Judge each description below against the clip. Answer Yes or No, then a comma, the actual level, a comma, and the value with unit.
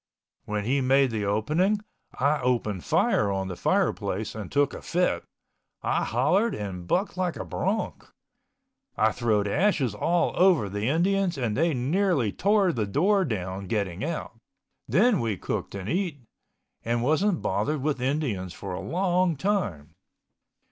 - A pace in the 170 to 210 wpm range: No, average, 150 wpm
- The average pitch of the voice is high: No, low, 135 Hz